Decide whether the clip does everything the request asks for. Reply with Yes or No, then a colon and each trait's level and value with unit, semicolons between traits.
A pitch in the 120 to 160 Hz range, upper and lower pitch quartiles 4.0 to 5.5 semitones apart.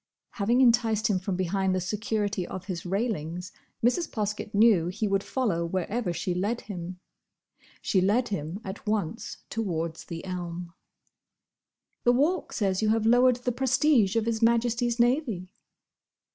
No: high, 210 Hz; average, 4.3 semitones